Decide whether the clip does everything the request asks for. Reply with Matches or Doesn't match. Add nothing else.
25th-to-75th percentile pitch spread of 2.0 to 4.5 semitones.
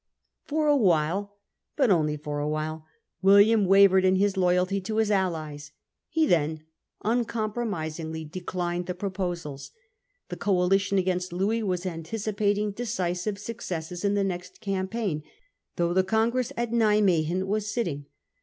Matches